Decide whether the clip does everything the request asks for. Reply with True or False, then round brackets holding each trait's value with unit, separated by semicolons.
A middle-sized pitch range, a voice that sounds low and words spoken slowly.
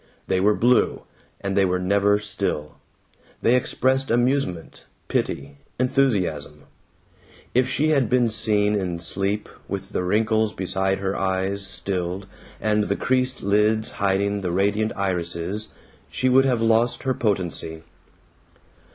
True (3.5 semitones; 100 Hz; 130 wpm)